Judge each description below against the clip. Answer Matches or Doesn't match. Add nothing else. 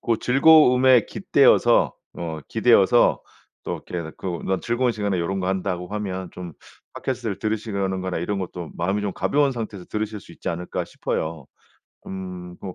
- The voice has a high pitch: Doesn't match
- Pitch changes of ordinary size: Matches